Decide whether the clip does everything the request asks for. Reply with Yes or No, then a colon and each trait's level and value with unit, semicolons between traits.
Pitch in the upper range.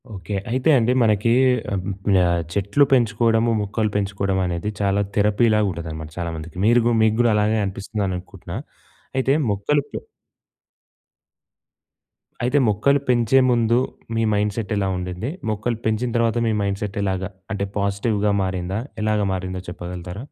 No: low, 105 Hz